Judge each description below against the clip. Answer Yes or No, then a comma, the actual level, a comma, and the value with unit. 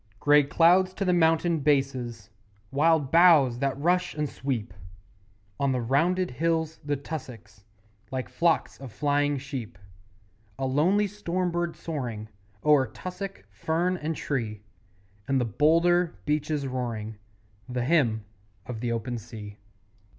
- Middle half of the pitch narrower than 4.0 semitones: No, average, 5.1 semitones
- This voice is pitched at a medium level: Yes, medium, 145 Hz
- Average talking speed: No, slow, 130 wpm